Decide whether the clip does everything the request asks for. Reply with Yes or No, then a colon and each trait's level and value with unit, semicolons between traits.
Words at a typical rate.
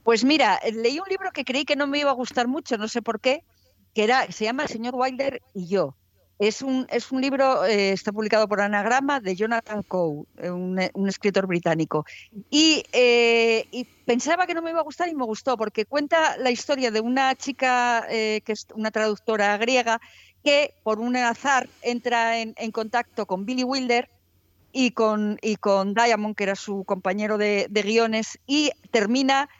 No: fast, 195 wpm